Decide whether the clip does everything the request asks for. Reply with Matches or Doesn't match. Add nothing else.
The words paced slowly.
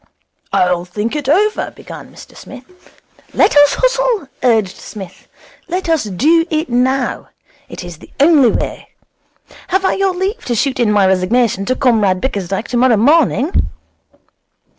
Doesn't match